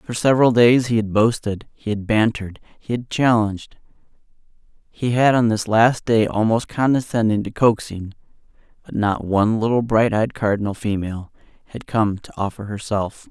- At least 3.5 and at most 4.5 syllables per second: No, 5.2 syllables/s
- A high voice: No, low, 110 Hz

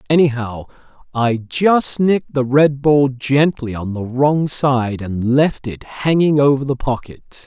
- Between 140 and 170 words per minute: Yes, average, 155 wpm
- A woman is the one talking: No, male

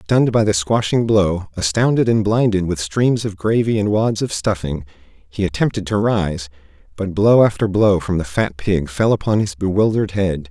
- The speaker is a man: Yes, male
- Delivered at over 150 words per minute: Yes, average, 190 wpm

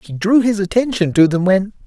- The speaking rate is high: Yes, fast, 225 wpm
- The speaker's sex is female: No, male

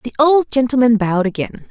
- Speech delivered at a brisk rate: No, average, 175 wpm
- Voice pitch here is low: No, high, 245 Hz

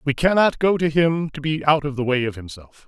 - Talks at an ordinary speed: No, fast, 270 wpm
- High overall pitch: No, medium, 150 Hz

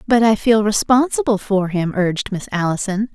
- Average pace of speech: Yes, average, 170 wpm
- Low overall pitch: No, high, 210 Hz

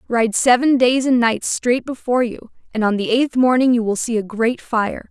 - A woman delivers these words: Yes, female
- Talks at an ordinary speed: No, fast, 225 wpm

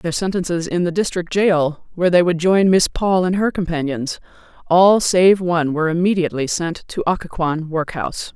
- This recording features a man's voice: No, female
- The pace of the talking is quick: No, average, 170 wpm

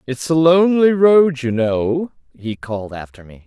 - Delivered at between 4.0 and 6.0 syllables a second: Yes, 4.5 syllables/s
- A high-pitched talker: No, medium, 140 Hz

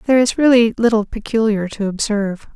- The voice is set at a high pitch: Yes, high, 220 Hz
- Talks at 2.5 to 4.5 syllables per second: No, 6.0 syllables/s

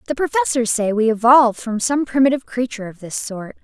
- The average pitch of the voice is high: Yes, high, 240 Hz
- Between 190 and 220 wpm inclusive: Yes, average, 200 wpm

